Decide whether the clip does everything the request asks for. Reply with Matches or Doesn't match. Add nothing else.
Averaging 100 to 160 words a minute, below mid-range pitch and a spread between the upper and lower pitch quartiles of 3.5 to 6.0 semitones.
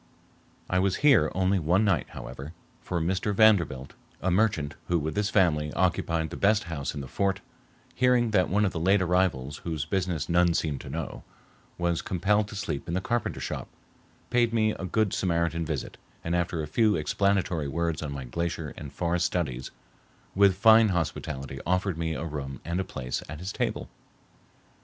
Doesn't match